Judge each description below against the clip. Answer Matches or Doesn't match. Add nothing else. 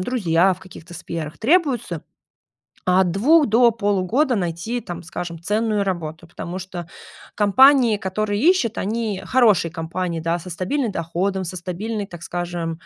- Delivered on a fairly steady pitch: Doesn't match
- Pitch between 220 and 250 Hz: Doesn't match